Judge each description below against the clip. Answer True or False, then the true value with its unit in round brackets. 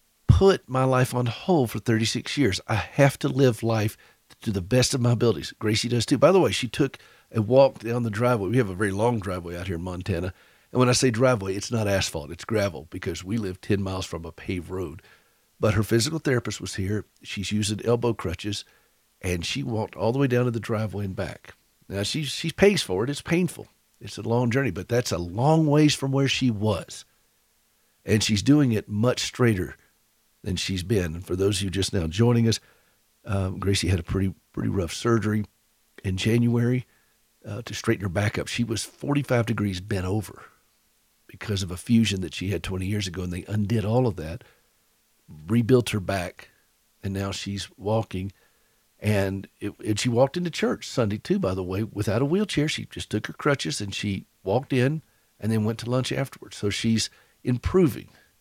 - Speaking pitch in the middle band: False (110 Hz)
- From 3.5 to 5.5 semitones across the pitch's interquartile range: True (4.0 semitones)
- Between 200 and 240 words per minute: True (205 wpm)